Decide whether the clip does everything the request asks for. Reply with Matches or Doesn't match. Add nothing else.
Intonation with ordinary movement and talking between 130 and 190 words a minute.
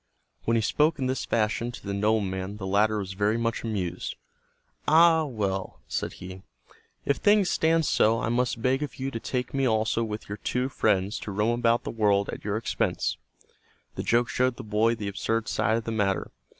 Doesn't match